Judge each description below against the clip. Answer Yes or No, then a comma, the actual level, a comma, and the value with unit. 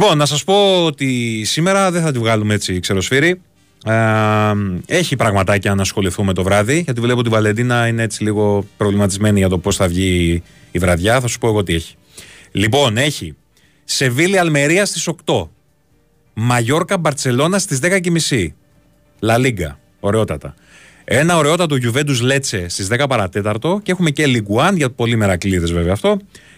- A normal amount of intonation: No, wide, 7.1 semitones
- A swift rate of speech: No, average, 155 wpm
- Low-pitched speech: Yes, low, 115 Hz